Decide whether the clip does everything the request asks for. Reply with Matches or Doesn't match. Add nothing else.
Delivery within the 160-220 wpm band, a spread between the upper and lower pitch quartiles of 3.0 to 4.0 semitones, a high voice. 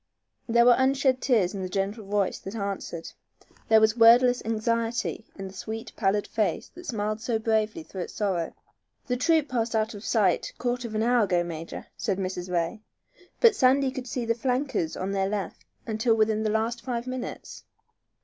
Matches